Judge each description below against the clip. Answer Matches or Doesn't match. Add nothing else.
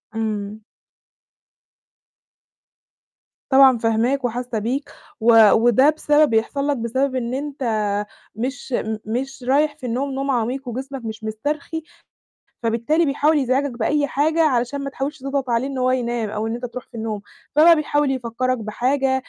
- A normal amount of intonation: Matches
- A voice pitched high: Matches